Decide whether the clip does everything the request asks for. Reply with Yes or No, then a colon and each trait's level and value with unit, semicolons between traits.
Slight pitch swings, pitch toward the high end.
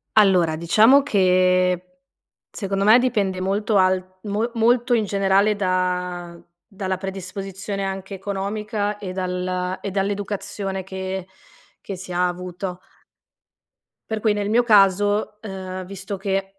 Yes: narrow, 1.9 semitones; high, 195 Hz